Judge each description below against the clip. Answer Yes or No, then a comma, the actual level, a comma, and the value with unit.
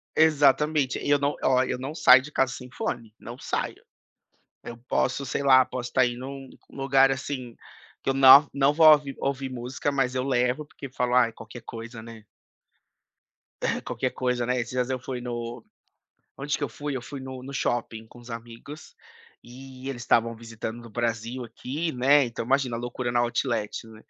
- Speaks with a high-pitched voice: No, low, 130 Hz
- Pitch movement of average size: No, narrow, 2.2 semitones